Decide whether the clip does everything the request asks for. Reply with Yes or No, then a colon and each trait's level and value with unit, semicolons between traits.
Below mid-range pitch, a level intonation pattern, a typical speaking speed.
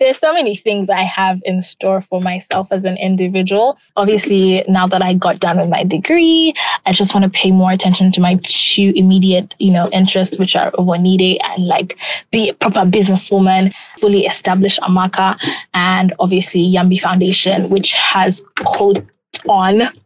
No: high, 190 Hz; narrow, 1.3 semitones; average, 165 wpm